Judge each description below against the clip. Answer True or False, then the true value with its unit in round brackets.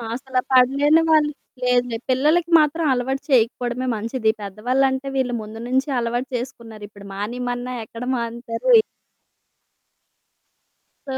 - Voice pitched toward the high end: True (250 Hz)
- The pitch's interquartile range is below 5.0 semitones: True (2.5 semitones)